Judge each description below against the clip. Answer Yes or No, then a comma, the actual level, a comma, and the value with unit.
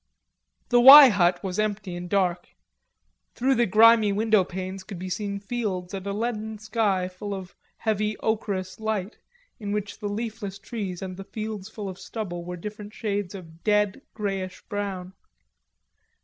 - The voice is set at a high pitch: Yes, high, 205 Hz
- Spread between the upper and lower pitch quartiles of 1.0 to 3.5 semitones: Yes, narrow, 2.5 semitones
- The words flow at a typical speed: Yes, average, 155 wpm